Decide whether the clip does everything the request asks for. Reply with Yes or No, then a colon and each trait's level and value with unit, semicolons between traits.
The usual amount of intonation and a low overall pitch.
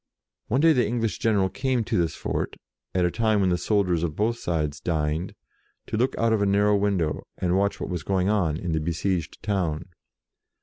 Yes: average, 4.1 semitones; very low, 95 Hz